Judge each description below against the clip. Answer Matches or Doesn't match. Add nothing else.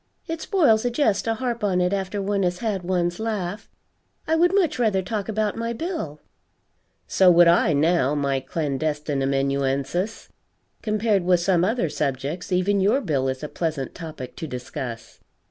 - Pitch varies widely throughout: Matches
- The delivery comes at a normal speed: Matches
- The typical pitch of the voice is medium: Matches